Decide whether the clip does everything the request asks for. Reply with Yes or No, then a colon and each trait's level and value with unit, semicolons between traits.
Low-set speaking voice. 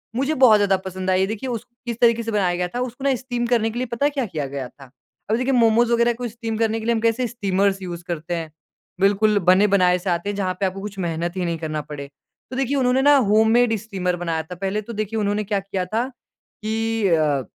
No: high, 205 Hz